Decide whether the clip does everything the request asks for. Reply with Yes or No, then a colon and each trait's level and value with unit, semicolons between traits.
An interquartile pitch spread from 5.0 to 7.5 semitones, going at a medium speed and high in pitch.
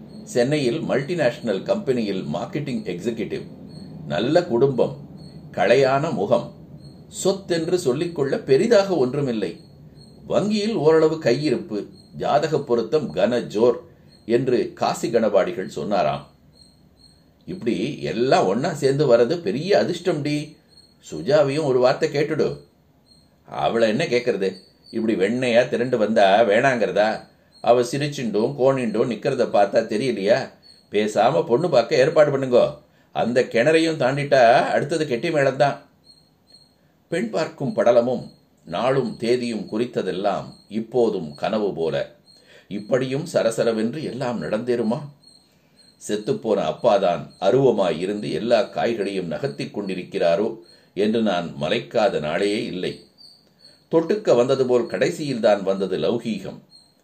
No: wide, 5.4 semitones; average, 95 wpm; low, 135 Hz